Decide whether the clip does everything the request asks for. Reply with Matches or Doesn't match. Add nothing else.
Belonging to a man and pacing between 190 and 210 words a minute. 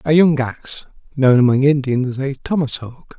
Doesn't match